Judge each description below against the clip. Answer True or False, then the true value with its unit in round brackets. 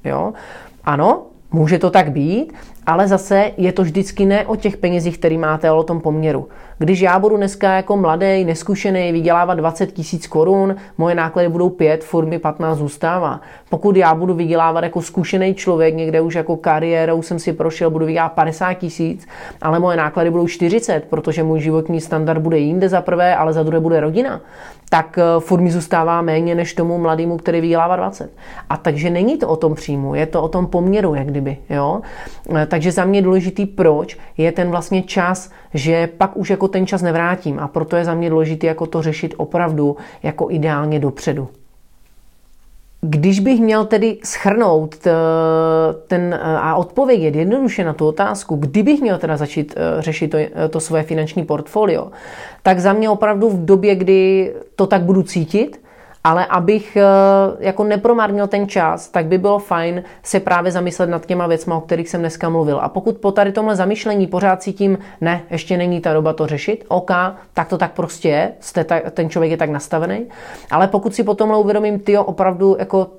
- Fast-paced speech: True (180 wpm)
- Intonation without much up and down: False (3.2 semitones)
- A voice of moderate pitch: True (175 Hz)